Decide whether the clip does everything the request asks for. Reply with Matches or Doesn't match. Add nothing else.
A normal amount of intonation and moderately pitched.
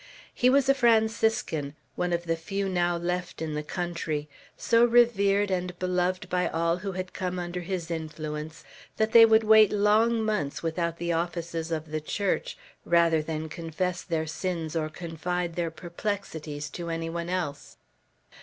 Matches